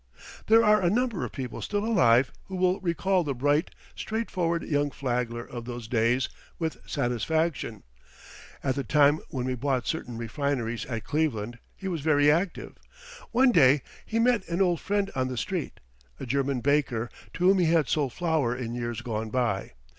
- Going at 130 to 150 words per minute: No, average, 175 wpm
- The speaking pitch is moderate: Yes, medium, 145 Hz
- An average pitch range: No, wide, 6.2 semitones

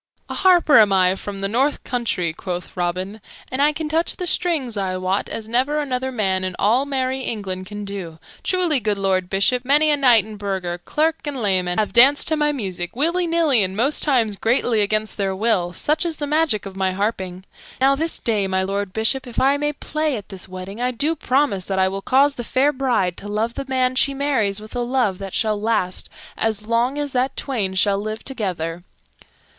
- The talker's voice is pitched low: No, high, 225 Hz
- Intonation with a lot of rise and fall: Yes, wide, 6.1 semitones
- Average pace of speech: No, fast, 210 wpm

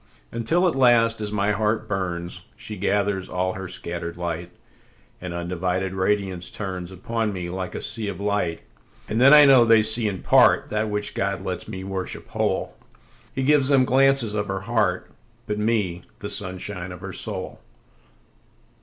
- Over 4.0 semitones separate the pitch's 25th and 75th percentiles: No, average, 3.6 semitones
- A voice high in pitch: No, low, 100 Hz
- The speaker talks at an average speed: Yes, average, 145 wpm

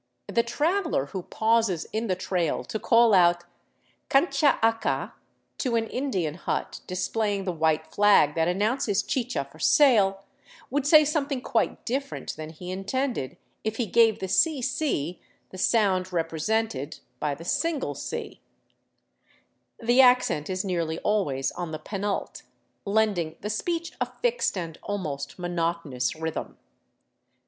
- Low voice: No, high, 200 Hz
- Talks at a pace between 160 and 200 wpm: No, average, 140 wpm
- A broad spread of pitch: Yes, wide, 6.1 semitones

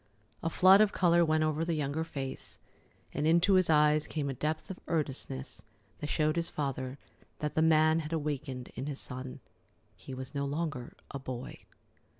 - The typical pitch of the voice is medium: Yes, medium, 150 Hz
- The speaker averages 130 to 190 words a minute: Yes, average, 175 wpm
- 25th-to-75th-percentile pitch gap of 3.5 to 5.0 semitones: No, average, 3.0 semitones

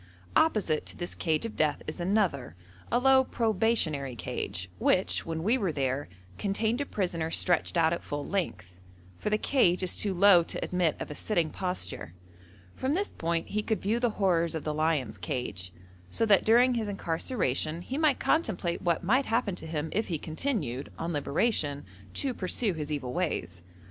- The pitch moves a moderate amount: No, wide, 6.1 semitones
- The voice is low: No, medium, 175 Hz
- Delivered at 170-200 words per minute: Yes, average, 180 wpm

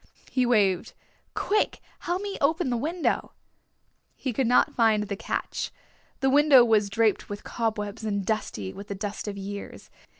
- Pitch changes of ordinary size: Yes, average, 4.6 semitones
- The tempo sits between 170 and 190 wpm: No, average, 160 wpm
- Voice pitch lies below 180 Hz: No, high, 220 Hz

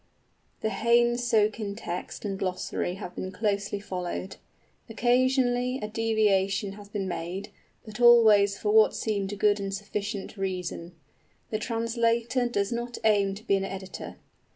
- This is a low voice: No, high, 210 Hz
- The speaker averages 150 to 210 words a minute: No, average, 140 wpm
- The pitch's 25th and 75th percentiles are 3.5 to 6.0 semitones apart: No, average, 2.9 semitones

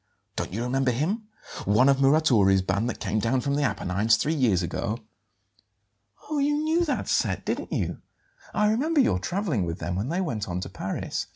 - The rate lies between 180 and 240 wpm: Yes, average, 190 wpm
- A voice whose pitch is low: Yes, low, 125 Hz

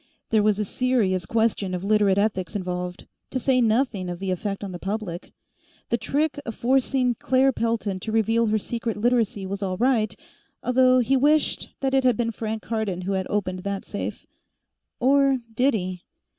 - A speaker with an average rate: Yes, average, 180 wpm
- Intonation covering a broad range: No, average, 4.4 semitones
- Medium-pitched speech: No, high, 220 Hz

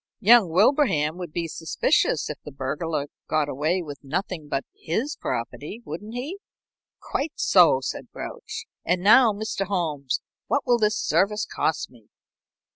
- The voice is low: No, medium, 175 Hz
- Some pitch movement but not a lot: No, wide, 6.4 semitones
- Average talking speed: Yes, average, 145 wpm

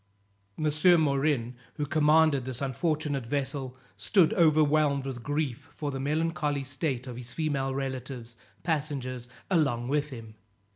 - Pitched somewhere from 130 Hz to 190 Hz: Yes, medium, 140 Hz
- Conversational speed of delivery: No, slow, 130 wpm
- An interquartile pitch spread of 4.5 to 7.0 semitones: No, average, 2.9 semitones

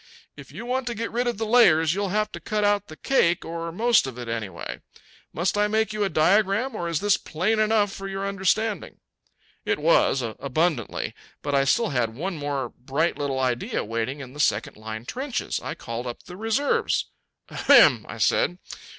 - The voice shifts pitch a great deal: Yes, wide, 8.1 semitones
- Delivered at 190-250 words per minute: Yes, average, 195 wpm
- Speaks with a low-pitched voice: No, medium, 180 Hz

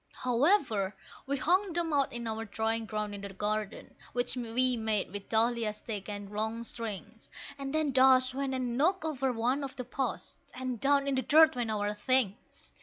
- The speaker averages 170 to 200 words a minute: Yes, average, 185 wpm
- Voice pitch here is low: No, high, 245 Hz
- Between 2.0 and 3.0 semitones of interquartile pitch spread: No, average, 4.0 semitones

